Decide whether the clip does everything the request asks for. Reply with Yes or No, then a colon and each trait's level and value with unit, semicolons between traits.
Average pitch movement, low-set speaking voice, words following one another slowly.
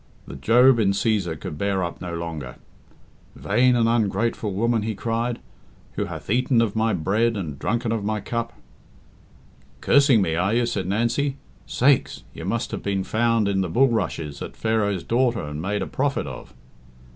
No: average, 3.7 semitones; low, 110 Hz; average, 175 wpm